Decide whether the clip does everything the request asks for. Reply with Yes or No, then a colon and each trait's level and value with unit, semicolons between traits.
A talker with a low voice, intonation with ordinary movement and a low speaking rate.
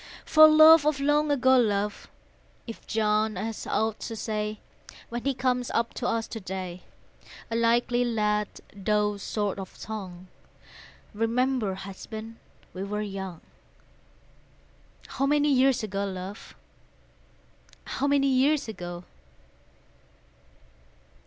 No: high, 220 Hz; average, 4.2 semitones; slow, 115 wpm